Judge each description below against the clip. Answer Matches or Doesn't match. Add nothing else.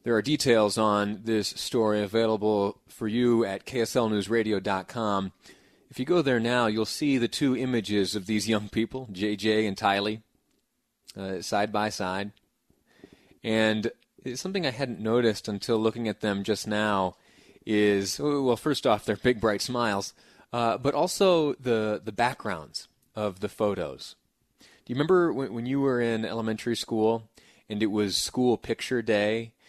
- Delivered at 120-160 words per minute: Matches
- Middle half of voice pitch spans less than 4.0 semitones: Matches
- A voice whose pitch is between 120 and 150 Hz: Doesn't match